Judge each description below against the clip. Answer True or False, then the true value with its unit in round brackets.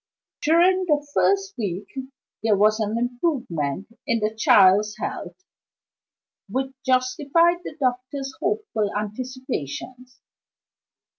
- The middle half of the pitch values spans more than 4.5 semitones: True (5.6 semitones)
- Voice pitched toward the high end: True (255 Hz)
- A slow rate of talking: True (95 wpm)